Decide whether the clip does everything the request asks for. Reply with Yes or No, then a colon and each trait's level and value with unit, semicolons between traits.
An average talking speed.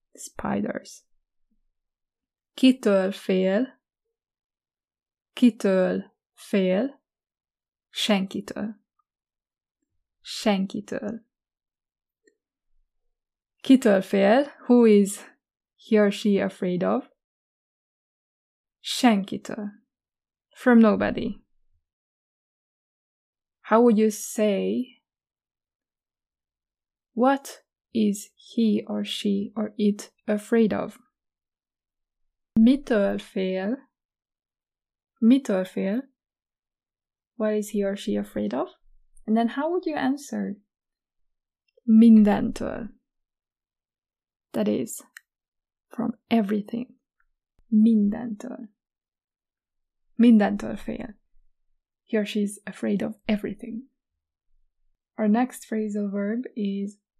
No: slow, 70 wpm